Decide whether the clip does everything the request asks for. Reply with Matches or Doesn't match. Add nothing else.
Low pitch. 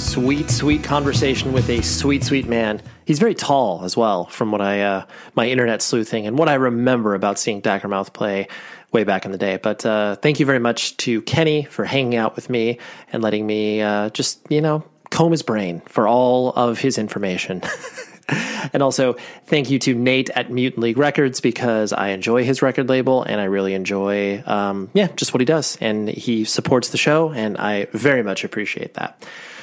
Matches